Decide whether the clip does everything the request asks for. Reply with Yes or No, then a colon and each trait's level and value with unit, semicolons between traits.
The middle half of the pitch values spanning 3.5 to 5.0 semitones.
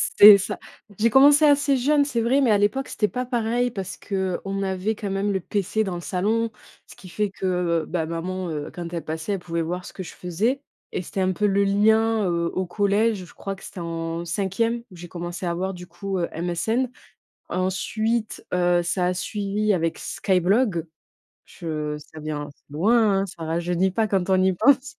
Yes: average, 3.9 semitones